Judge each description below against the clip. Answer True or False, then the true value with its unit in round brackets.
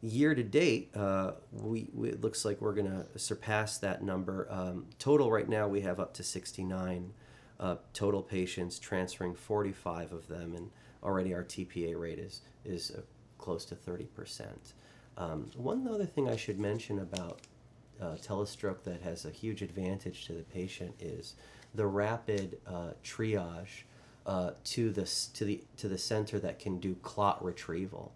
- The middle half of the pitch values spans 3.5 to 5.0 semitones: False (3.1 semitones)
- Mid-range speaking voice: False (100 Hz)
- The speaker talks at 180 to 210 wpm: False (165 wpm)